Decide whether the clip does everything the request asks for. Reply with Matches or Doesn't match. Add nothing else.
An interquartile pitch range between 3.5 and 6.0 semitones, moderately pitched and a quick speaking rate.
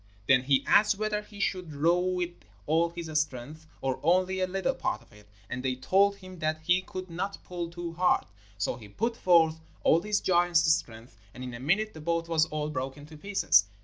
Matches